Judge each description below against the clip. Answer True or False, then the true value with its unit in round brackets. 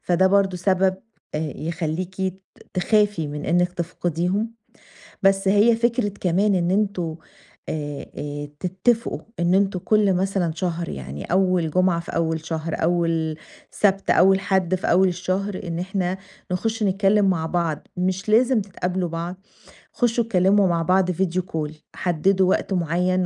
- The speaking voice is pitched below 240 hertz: True (185 Hz)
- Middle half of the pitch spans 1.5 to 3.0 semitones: True (2.5 semitones)